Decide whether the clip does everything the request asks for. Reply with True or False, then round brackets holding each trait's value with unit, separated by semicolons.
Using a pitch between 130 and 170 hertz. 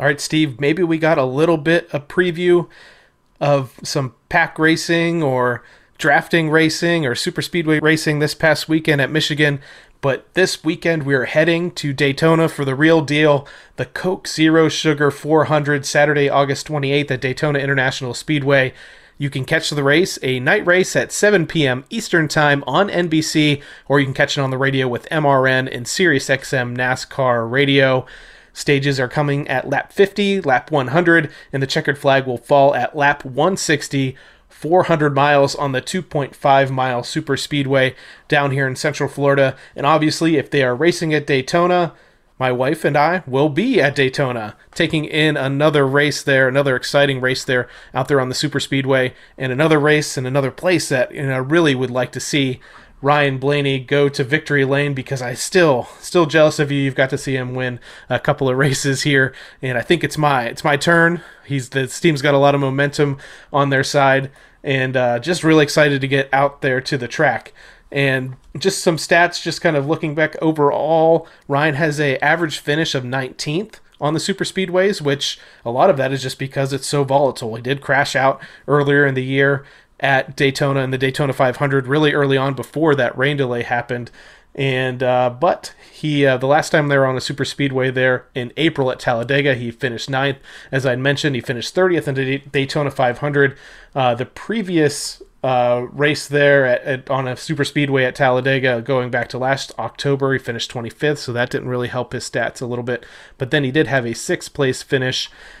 True (140 Hz)